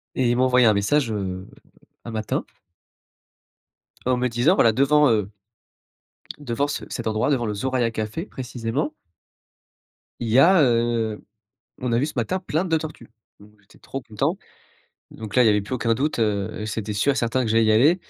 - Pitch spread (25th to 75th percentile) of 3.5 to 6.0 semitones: Yes, average, 3.9 semitones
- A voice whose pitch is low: Yes, low, 120 Hz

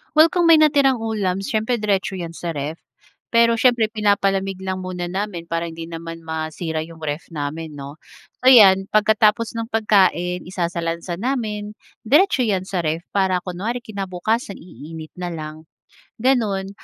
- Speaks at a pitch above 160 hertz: Yes, high, 190 Hz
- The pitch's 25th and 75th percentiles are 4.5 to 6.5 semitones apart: Yes, average, 4.8 semitones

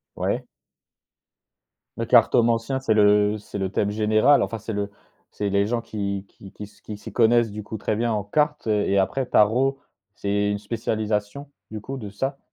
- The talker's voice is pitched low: Yes, low, 105 Hz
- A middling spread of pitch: No, narrow, 2.3 semitones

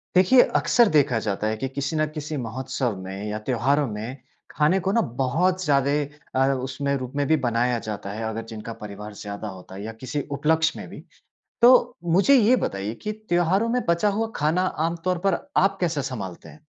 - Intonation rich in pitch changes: Yes, wide, 7.6 semitones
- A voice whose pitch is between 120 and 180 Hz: Yes, medium, 140 Hz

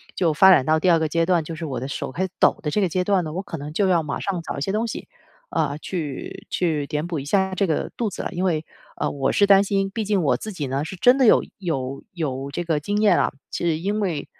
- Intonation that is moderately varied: Yes, average, 4.3 semitones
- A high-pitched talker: No, medium, 170 Hz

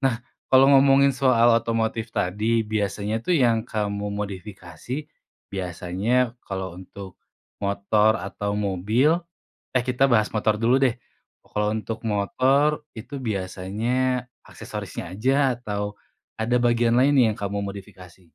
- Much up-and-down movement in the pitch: No, average, 3.7 semitones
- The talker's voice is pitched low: Yes, low, 110 Hz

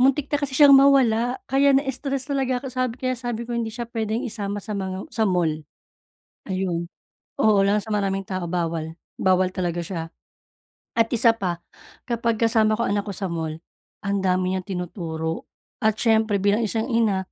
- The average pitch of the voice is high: Yes, high, 215 Hz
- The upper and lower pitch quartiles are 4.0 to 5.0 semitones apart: Yes, average, 4.3 semitones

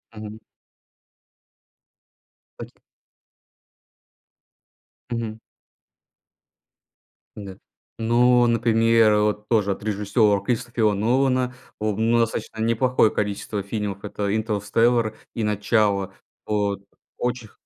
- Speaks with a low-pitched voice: Yes, low, 110 Hz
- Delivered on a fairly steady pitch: Yes, narrow, 2.1 semitones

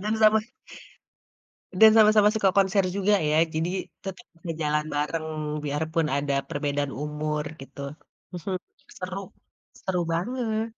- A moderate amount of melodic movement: No, wide, 5.7 semitones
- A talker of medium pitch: Yes, medium, 180 Hz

